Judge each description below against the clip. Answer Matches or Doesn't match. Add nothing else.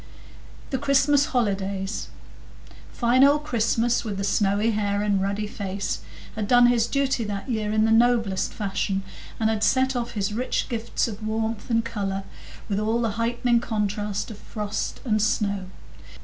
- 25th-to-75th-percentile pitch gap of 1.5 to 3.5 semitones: Matches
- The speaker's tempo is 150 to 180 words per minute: Matches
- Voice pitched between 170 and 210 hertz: Doesn't match